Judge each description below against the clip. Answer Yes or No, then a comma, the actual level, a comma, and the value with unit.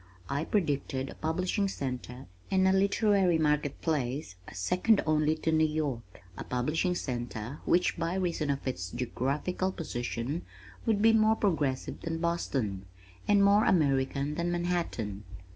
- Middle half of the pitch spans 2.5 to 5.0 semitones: No, wide, 5.6 semitones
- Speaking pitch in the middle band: Yes, medium, 155 Hz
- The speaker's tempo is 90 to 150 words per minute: Yes, average, 140 wpm